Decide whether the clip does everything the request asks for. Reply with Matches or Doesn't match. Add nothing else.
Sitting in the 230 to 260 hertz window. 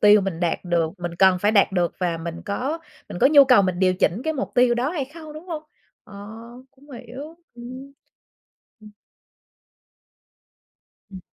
Doesn't match